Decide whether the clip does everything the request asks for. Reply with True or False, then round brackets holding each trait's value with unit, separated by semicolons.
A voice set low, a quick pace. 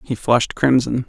False (125 Hz; 165 wpm)